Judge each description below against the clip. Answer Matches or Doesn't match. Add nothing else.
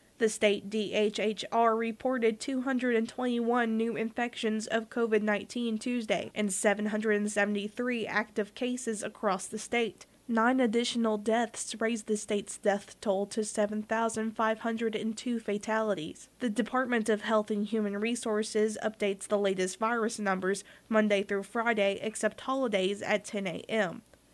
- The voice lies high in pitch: Matches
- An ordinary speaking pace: Doesn't match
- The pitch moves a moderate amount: Doesn't match